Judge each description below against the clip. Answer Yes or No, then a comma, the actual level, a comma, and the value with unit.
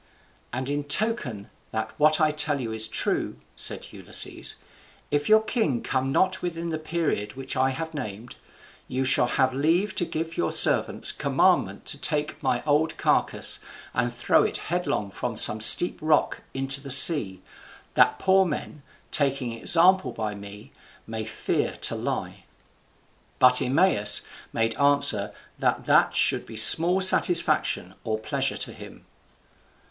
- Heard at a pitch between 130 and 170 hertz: Yes, medium, 140 Hz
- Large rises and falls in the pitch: Yes, wide, 6.0 semitones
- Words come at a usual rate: Yes, average, 150 wpm